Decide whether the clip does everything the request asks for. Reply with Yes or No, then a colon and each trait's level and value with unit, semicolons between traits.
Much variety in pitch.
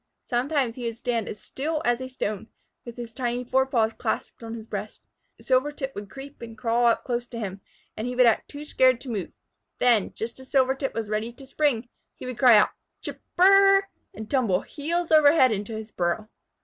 No: average, 3.2 semitones